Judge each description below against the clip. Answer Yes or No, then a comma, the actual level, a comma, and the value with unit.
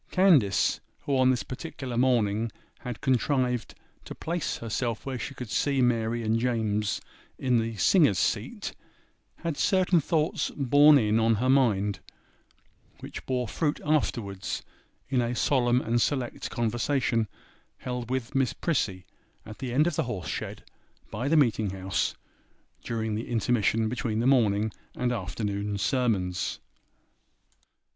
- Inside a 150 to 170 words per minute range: No, slow, 135 wpm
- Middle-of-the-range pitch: No, low, 120 Hz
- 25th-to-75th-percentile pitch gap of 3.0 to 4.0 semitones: Yes, average, 3.5 semitones